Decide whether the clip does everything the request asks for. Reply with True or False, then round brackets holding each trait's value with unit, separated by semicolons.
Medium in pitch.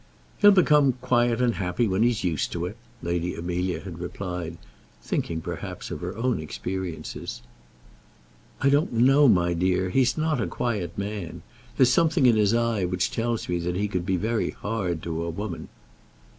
False (100 Hz)